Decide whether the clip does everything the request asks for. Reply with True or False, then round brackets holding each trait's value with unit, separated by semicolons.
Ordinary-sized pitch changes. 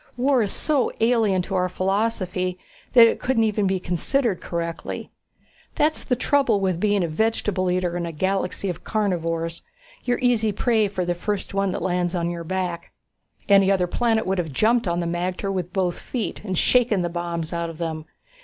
True (4.0 semitones)